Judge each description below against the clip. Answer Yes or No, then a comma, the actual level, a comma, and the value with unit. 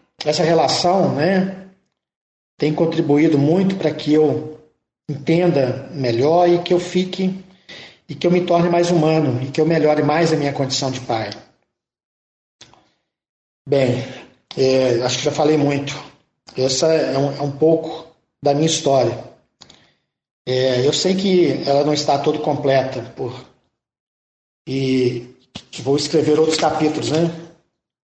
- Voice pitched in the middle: Yes, medium, 150 Hz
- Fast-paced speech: No, average, 135 wpm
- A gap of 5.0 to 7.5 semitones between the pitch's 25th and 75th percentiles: No, average, 3.5 semitones